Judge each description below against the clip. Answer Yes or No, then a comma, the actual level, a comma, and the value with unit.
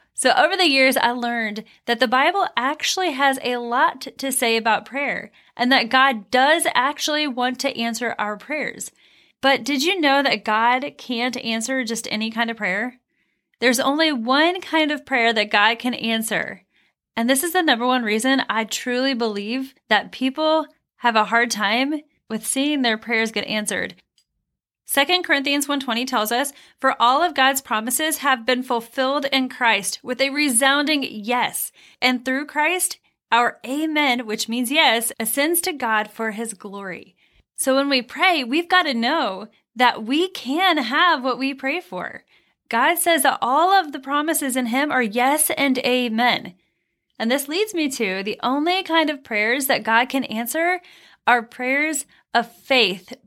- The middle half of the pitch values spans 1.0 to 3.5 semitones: No, average, 4.0 semitones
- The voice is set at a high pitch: Yes, very high, 260 Hz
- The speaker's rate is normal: Yes, average, 170 wpm